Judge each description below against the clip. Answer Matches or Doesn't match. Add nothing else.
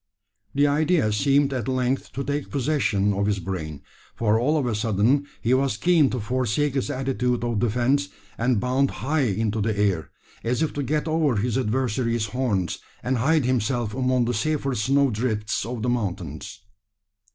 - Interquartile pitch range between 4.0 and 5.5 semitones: Matches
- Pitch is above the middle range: Doesn't match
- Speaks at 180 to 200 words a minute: Doesn't match